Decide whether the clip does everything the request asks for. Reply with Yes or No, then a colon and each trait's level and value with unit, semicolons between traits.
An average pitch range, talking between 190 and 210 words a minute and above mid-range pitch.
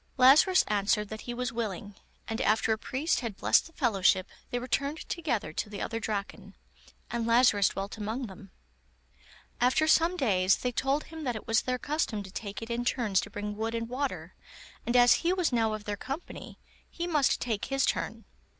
Yes: average, 4.4 semitones; average, 195 wpm; high, 235 Hz